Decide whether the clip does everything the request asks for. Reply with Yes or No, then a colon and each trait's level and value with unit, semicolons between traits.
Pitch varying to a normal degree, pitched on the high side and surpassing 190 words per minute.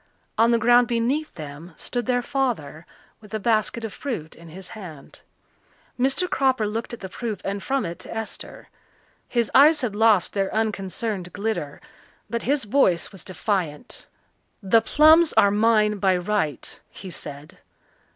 No: average, 4.4 semitones; high, 215 Hz; average, 155 wpm